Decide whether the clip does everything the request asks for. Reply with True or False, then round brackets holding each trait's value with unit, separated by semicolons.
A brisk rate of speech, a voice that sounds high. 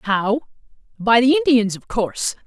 False (145 wpm; 230 Hz)